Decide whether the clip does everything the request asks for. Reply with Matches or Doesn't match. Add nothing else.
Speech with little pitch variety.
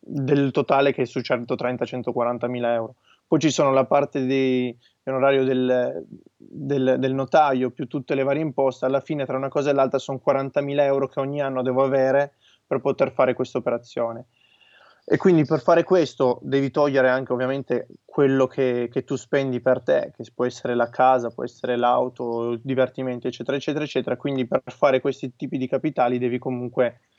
Matches